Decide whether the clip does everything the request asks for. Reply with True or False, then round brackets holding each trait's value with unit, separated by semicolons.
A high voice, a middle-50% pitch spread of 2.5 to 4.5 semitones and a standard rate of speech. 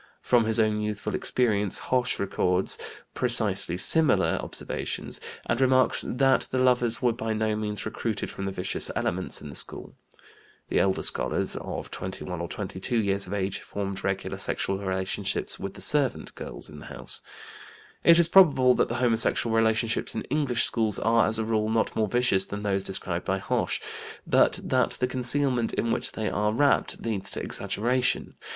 False (110 Hz; 4.0 semitones; 170 wpm)